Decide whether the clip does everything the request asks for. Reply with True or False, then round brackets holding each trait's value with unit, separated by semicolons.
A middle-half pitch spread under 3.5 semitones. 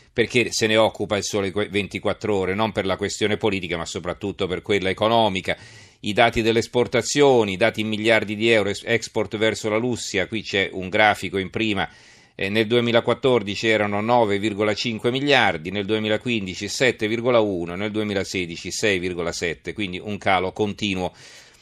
True (2.5 semitones)